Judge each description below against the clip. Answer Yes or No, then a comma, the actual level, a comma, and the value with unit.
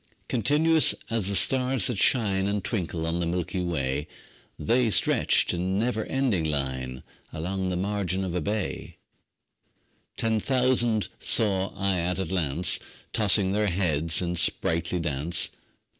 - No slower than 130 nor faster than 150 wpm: Yes, average, 140 wpm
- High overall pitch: No, very low, 95 Hz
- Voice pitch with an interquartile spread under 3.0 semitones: No, average, 4.5 semitones